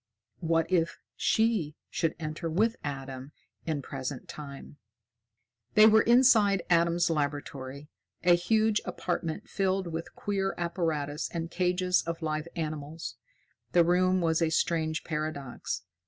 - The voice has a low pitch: No, medium, 165 Hz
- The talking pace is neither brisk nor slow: No, slow, 125 wpm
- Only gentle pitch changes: No, average, 3.2 semitones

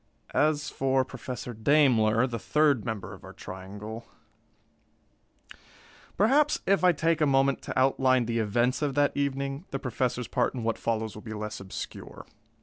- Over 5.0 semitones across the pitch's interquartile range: No, average, 4.2 semitones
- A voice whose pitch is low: Yes, low, 130 Hz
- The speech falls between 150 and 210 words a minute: Yes, average, 155 wpm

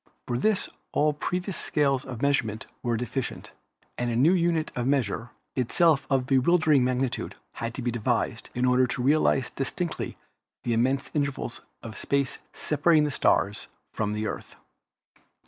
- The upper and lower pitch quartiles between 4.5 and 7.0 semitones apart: No, average, 3.7 semitones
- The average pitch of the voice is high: No, low, 130 Hz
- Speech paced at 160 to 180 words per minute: No, average, 150 wpm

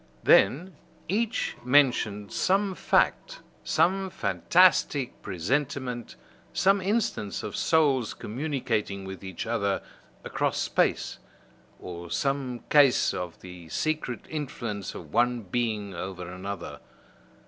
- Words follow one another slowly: Yes, slow, 105 wpm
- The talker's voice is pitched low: Yes, low, 120 Hz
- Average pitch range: No, wide, 7.7 semitones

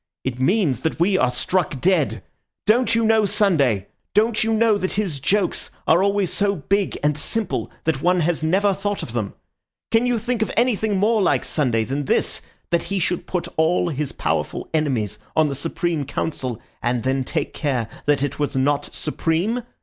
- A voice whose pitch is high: No, medium, 170 Hz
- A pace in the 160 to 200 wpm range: Yes, average, 185 wpm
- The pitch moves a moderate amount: No, wide, 6.7 semitones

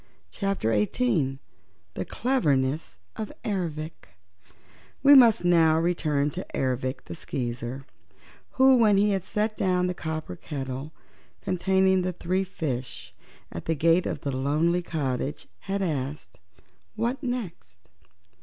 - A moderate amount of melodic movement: No, wide, 6.3 semitones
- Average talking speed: No, slow, 125 wpm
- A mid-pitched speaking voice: Yes, medium, 165 Hz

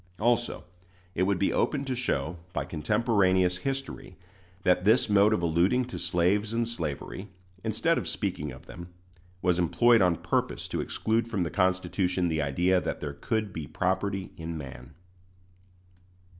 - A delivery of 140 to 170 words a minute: Yes, average, 155 wpm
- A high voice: No, very low, 95 Hz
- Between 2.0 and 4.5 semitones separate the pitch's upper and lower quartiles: Yes, average, 4.2 semitones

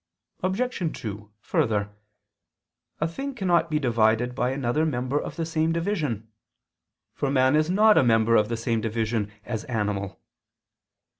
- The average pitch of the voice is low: Yes, low, 125 Hz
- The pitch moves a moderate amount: No, wide, 6.6 semitones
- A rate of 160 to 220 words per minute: No, average, 145 wpm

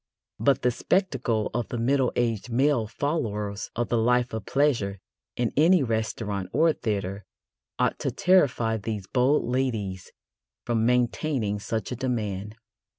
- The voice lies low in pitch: Yes, low, 120 Hz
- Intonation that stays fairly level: No, average, 3.7 semitones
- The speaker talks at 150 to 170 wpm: No, average, 140 wpm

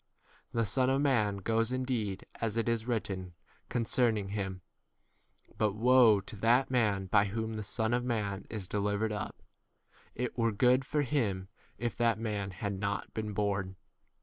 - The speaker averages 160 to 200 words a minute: Yes, average, 165 wpm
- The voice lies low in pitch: Yes, low, 110 Hz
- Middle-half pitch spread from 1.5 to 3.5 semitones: Yes, average, 2.9 semitones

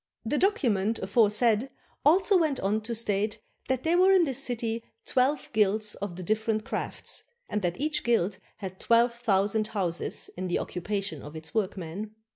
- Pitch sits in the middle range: No, high, 215 Hz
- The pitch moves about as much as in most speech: Yes, average, 4.0 semitones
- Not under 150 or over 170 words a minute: Yes, average, 165 wpm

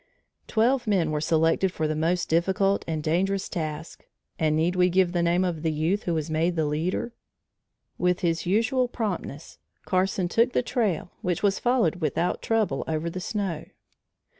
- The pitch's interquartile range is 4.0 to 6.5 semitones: No, average, 3.5 semitones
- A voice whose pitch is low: No, medium, 175 Hz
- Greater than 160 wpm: Yes, average, 170 wpm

